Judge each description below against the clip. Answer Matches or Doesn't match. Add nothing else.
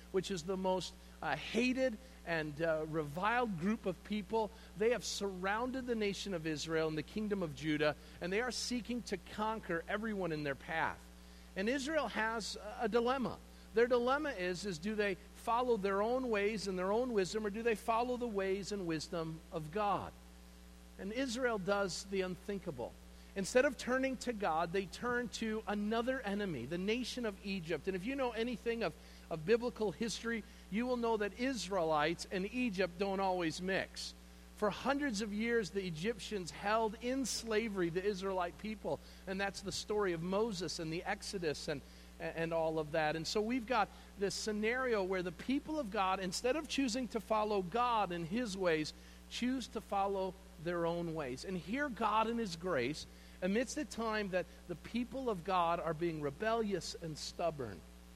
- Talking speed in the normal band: Matches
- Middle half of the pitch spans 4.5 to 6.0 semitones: Matches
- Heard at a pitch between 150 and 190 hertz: Doesn't match